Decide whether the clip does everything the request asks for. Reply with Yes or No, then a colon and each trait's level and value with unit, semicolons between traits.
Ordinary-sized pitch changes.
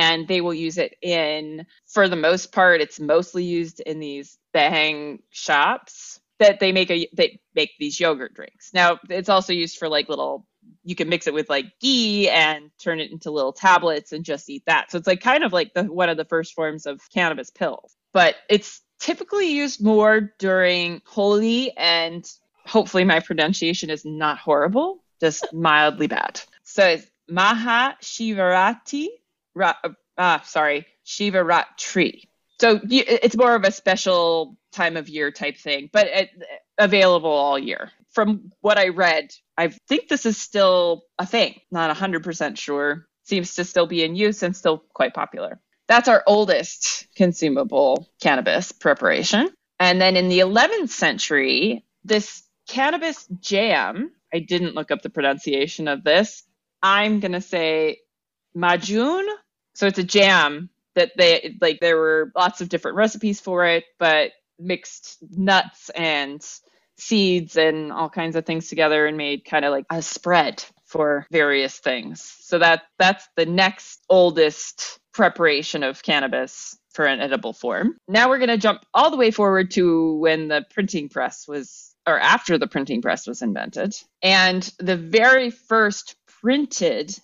Yes: average, 4.7 semitones